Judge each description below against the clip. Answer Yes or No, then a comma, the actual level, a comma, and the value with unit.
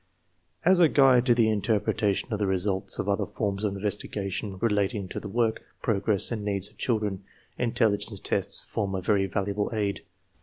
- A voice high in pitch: No, low, 105 Hz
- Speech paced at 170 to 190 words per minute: Yes, average, 175 wpm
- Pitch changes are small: Yes, narrow, 2.2 semitones